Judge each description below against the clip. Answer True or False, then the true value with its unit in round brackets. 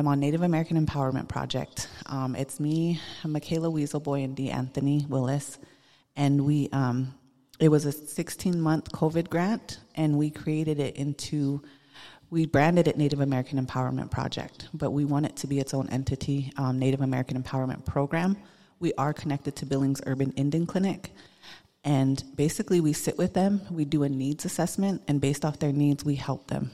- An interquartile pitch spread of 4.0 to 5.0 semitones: False (2.7 semitones)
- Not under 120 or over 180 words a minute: True (175 wpm)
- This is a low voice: False (145 Hz)